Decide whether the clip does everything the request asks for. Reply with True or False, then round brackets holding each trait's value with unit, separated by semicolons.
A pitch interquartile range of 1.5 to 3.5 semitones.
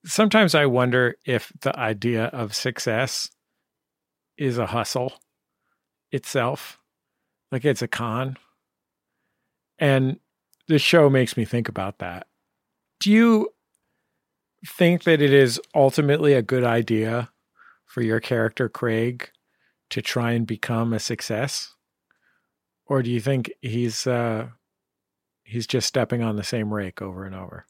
True (3.2 semitones)